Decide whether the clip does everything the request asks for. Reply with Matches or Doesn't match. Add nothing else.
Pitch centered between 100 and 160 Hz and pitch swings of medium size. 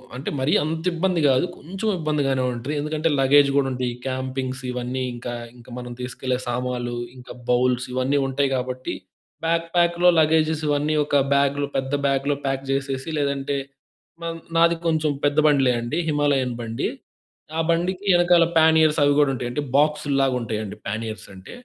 Matches